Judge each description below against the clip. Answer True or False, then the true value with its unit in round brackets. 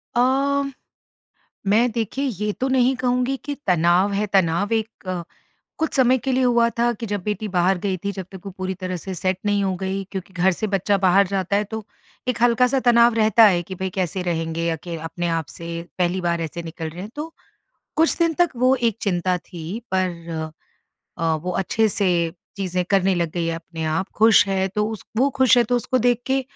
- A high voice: True (195 Hz)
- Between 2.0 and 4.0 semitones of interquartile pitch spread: False (4.9 semitones)